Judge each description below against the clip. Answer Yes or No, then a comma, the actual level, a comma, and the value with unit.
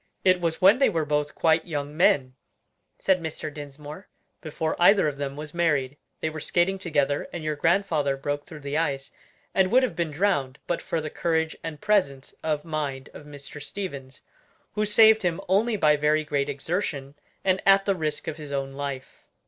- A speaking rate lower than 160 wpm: No, average, 190 wpm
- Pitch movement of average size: Yes, average, 3.8 semitones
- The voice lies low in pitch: No, medium, 155 Hz